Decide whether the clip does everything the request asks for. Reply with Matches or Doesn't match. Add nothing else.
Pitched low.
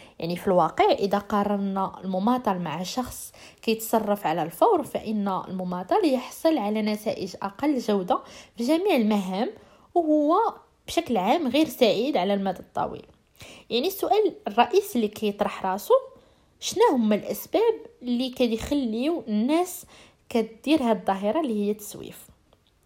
Doesn't match